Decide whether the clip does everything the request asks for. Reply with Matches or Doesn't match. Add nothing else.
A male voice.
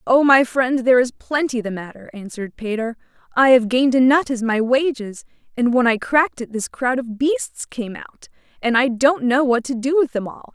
Doesn't match